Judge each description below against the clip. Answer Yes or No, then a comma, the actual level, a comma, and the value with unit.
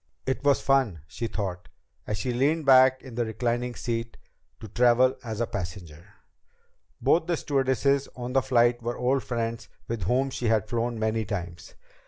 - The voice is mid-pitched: No, low, 120 Hz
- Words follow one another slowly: No, average, 170 wpm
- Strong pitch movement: No, average, 3.0 semitones